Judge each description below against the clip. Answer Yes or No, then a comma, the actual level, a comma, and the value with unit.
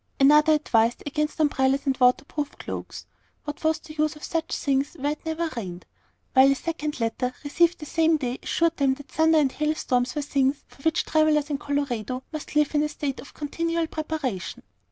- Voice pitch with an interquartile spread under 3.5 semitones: Yes, average, 2.7 semitones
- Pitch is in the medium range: No, very high, 295 Hz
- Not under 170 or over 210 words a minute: Yes, average, 195 wpm